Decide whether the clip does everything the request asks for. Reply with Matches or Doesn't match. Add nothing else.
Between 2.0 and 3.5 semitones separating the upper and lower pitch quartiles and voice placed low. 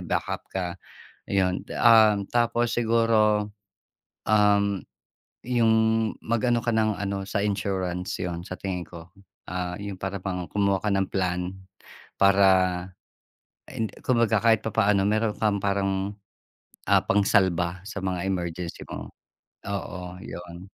Matches